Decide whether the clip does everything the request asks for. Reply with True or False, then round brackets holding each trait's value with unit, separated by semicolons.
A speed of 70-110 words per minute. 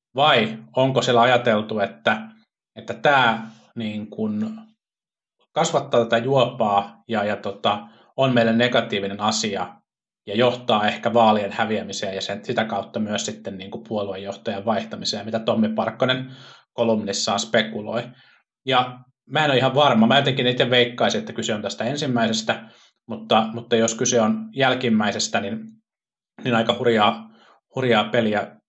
False (135 wpm)